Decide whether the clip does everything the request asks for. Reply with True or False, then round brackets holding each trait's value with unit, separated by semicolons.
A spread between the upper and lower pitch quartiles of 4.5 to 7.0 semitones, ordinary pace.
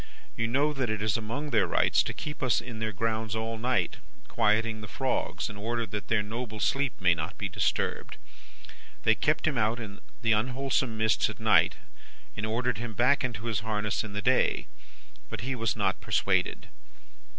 False (2.5 semitones; 185 wpm)